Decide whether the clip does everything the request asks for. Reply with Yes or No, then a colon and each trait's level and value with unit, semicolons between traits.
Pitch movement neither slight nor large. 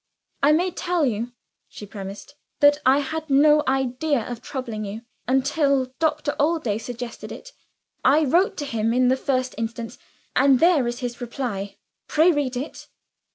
Yes: average, 3.9 semitones